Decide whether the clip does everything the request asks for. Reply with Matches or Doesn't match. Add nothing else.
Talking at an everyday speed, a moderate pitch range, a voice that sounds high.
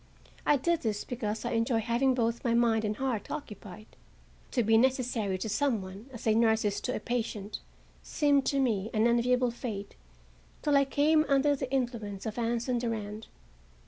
Matches